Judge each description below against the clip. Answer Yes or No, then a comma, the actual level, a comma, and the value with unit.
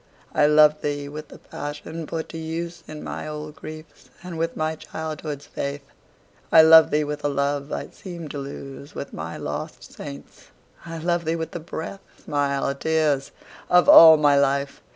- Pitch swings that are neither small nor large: No, narrow, 2.1 semitones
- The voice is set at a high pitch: No, medium, 150 Hz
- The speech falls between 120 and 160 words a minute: No, average, 175 wpm